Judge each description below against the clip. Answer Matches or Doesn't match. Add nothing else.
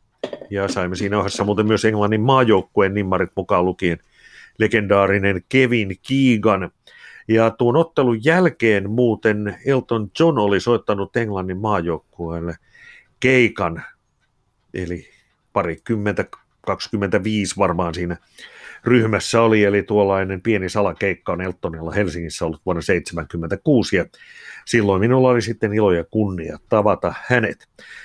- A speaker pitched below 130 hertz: Matches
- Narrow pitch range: Doesn't match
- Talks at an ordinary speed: Matches